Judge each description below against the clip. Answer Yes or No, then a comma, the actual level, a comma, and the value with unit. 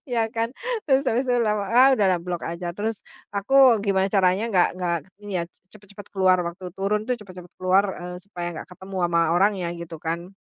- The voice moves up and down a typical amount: Yes, average, 3.2 semitones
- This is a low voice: No, high, 190 Hz